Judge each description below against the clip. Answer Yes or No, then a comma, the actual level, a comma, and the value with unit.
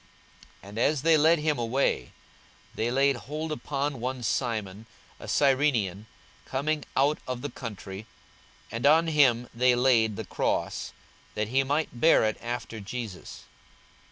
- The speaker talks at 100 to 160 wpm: Yes, average, 145 wpm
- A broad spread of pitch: No, average, 4.3 semitones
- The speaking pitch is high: No, low, 125 Hz